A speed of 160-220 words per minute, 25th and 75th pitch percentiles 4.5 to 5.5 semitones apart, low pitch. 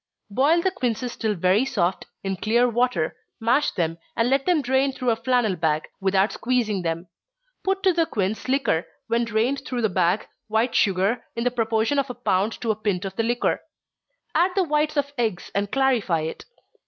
No: average, 190 wpm; average, 5.2 semitones; high, 230 Hz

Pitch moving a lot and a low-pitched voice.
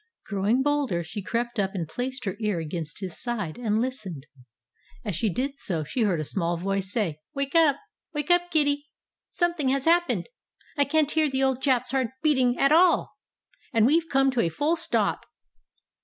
No: wide, 6.8 semitones; very high, 250 Hz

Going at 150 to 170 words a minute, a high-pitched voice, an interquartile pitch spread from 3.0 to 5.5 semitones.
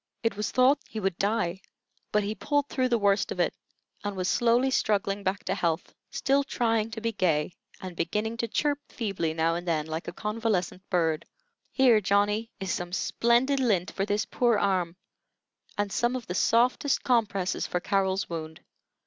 No: average, 180 wpm; high, 205 Hz; average, 4.2 semitones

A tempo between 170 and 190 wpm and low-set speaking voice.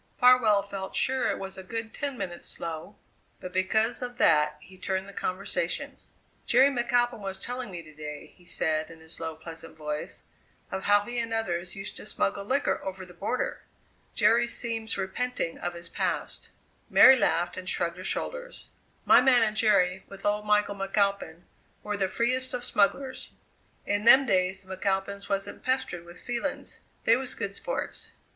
No: average, 175 wpm; high, 200 Hz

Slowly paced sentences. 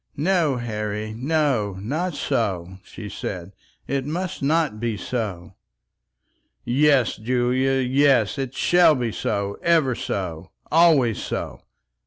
Yes: slow, 115 wpm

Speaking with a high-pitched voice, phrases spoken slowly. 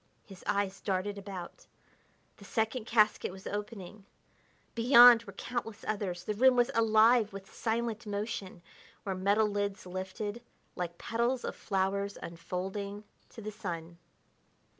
Yes: high, 205 Hz; slow, 130 wpm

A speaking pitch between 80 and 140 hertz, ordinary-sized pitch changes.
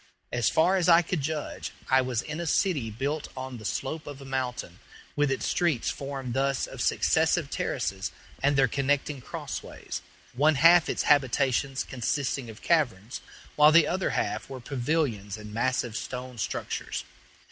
Yes: low, 135 Hz; average, 3.4 semitones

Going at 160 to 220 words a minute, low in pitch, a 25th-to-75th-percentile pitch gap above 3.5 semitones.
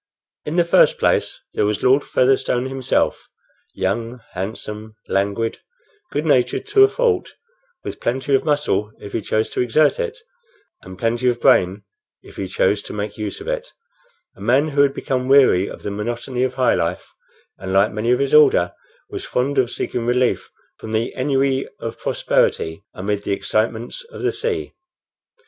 Yes: average, 170 wpm; low, 125 Hz; average, 4.9 semitones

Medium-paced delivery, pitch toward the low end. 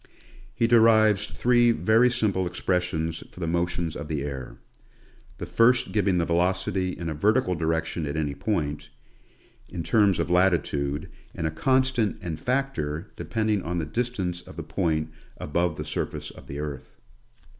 Yes: average, 160 wpm; very low, 90 Hz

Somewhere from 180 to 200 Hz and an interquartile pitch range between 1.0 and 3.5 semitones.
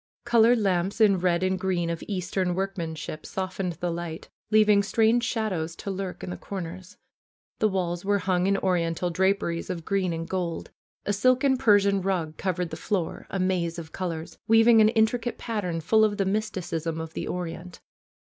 Yes: medium, 185 Hz; average, 3.2 semitones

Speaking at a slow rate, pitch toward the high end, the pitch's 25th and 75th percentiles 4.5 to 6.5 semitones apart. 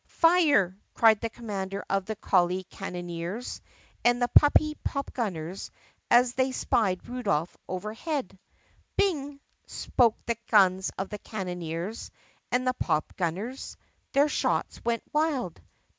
Yes: slow, 120 wpm; high, 220 Hz; wide, 5.5 semitones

